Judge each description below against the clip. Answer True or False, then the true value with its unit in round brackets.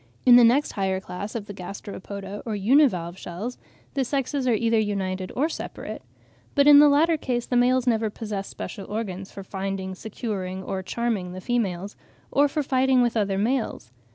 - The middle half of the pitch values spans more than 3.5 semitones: True (4.7 semitones)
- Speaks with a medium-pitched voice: False (215 Hz)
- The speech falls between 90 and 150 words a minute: False (180 wpm)